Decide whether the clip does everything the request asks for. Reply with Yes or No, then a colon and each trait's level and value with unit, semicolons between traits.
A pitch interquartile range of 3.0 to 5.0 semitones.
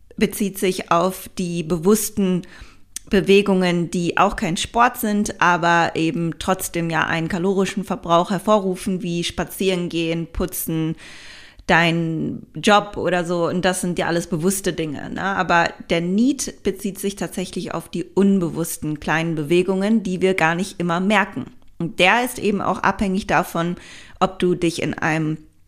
No: narrow, 2.6 semitones